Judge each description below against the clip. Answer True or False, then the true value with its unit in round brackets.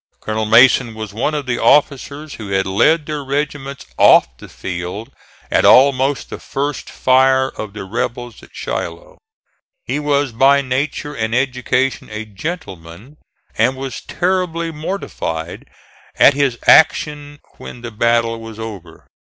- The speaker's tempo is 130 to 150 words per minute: True (140 wpm)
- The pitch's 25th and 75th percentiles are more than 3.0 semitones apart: True (4.7 semitones)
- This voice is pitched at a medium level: False (130 Hz)